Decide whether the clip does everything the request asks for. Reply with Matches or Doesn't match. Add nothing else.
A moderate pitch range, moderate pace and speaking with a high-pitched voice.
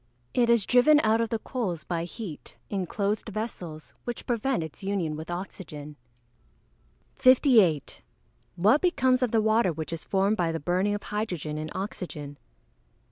Doesn't match